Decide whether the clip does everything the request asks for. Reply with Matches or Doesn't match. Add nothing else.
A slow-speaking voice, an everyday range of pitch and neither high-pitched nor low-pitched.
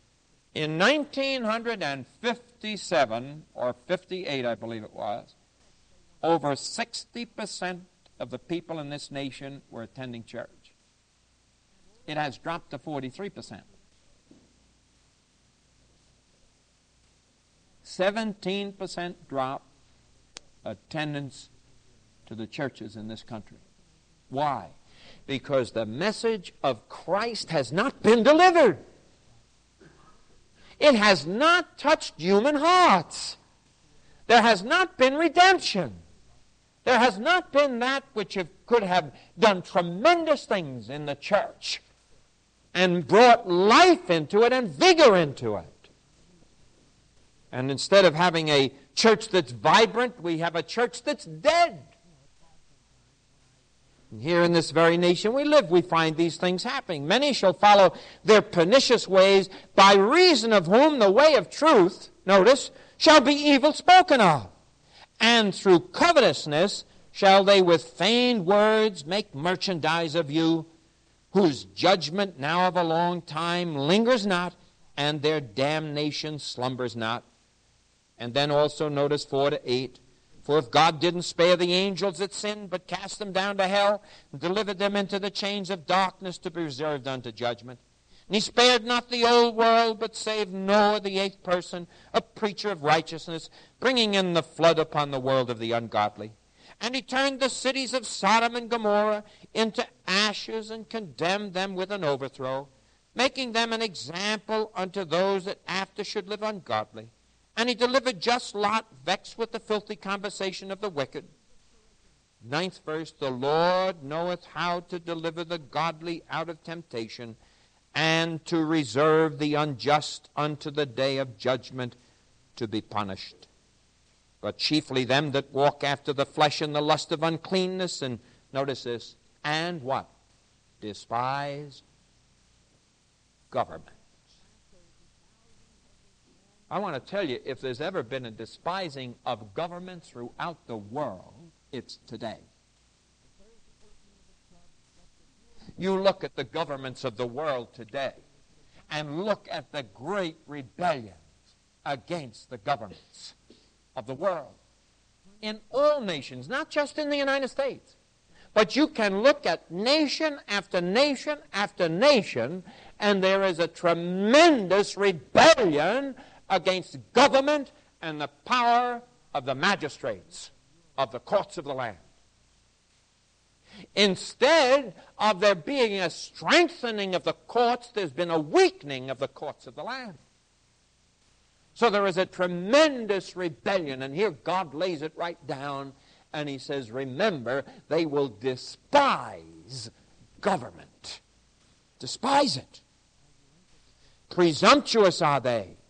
Doesn't match